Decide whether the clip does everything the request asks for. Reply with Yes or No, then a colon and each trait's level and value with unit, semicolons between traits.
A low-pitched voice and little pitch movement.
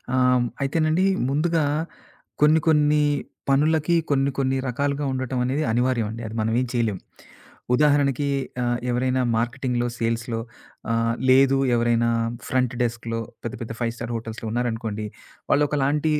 No: low, 130 Hz; average, 3.5 semitones